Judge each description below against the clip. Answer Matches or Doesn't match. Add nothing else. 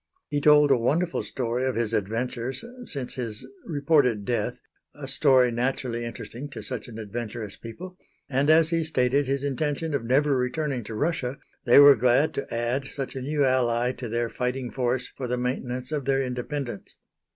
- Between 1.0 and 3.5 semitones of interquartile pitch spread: Matches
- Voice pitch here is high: Doesn't match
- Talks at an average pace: Matches